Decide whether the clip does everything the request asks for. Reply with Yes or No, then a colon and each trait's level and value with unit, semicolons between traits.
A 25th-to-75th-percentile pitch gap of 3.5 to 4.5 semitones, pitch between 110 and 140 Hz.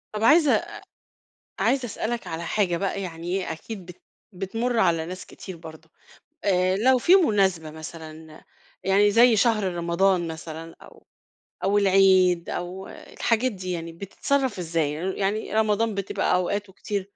No: average, 3.8 semitones; high, 190 Hz